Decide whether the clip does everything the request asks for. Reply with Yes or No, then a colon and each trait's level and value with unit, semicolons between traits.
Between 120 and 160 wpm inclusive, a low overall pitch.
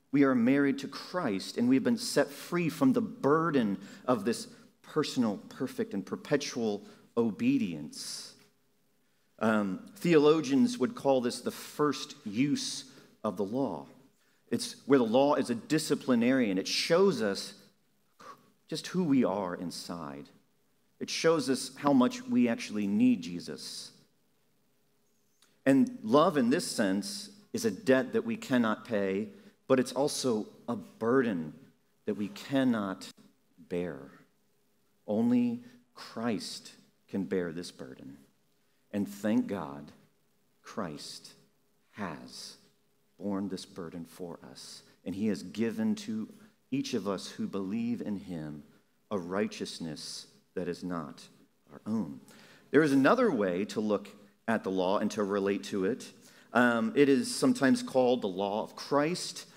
No: slow, 135 wpm; medium, 145 Hz